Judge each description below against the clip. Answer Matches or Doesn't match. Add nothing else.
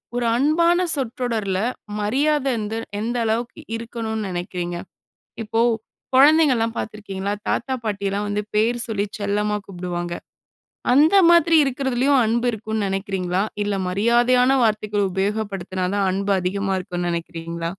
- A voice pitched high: Matches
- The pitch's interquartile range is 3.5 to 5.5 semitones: Matches